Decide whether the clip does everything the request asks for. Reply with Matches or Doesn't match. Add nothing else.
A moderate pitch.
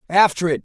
Matches